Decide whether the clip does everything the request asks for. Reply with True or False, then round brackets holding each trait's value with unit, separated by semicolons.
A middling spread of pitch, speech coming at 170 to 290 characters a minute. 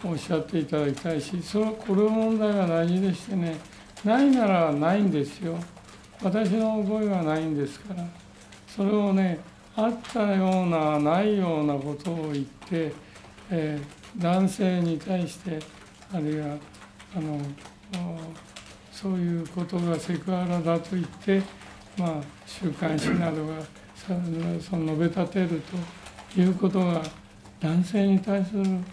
True (3.5 semitones; 265 characters per minute)